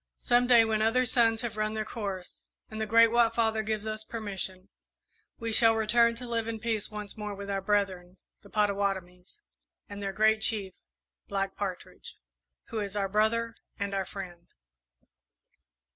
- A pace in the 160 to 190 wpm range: Yes, average, 165 wpm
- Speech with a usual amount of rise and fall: No, narrow, 2.3 semitones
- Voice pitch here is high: Yes, high, 215 Hz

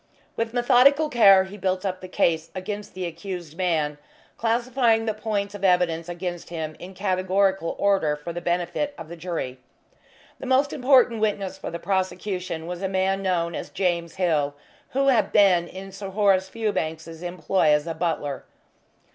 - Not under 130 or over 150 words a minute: No, average, 165 wpm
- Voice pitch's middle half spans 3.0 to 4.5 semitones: Yes, average, 3.3 semitones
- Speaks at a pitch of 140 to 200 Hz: Yes, medium, 185 Hz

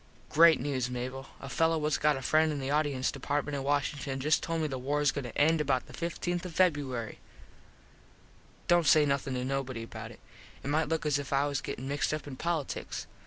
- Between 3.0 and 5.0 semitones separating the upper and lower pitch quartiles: No, narrow, 2.6 semitones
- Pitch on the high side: No, medium, 145 Hz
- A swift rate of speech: Yes, fast, 215 wpm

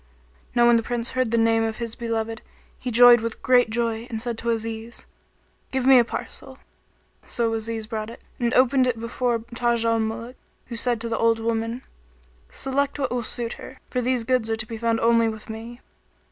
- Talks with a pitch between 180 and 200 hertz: No, high, 230 Hz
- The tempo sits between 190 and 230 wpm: Yes, fast, 205 wpm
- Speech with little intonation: Yes, narrow, 1.4 semitones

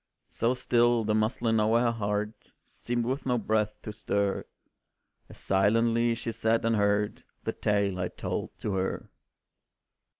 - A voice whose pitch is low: Yes, low, 110 Hz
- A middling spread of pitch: No, narrow, 2.2 semitones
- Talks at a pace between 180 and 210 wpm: No, average, 145 wpm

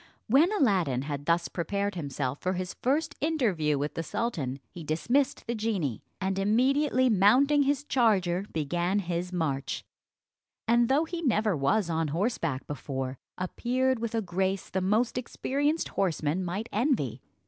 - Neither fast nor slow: Yes, average, 150 wpm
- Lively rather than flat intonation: Yes, wide, 7.2 semitones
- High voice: Yes, high, 195 Hz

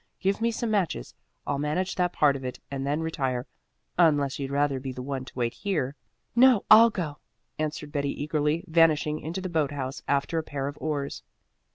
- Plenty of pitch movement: No, average, 3.4 semitones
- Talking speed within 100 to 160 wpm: No, average, 195 wpm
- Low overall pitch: No, medium, 150 Hz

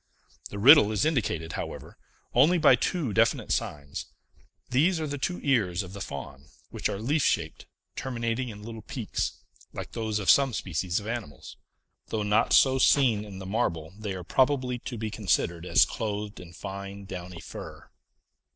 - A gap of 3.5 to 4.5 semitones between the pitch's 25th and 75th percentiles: No, average, 5.2 semitones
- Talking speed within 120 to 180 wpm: Yes, average, 170 wpm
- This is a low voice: Yes, low, 105 Hz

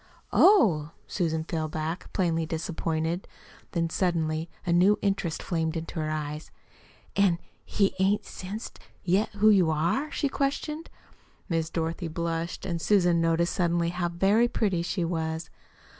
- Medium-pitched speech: Yes, medium, 170 Hz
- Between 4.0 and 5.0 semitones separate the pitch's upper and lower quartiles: No, average, 3.1 semitones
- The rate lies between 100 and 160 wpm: Yes, average, 140 wpm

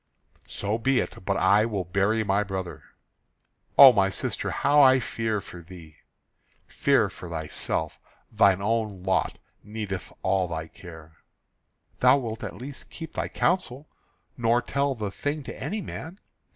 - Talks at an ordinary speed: Yes, average, 150 wpm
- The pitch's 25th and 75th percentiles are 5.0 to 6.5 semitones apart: Yes, wide, 5.5 semitones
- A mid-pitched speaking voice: No, low, 105 Hz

